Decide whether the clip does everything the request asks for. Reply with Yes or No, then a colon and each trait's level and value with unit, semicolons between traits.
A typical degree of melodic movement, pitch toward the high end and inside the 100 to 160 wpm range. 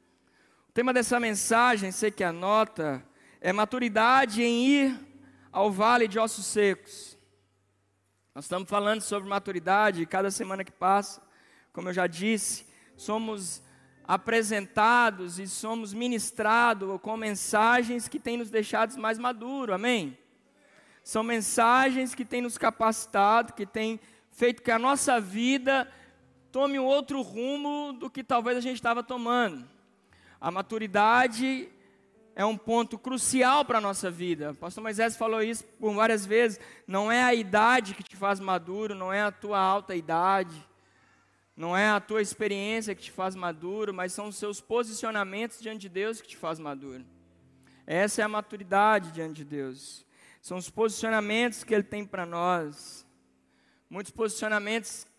Yes: average, 3.7 semitones; high, 215 Hz; average, 150 wpm